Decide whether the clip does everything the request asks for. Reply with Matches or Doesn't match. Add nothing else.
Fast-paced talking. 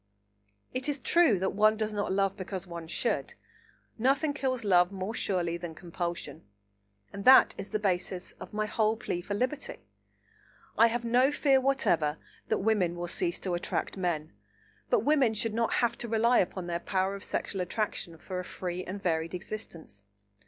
Doesn't match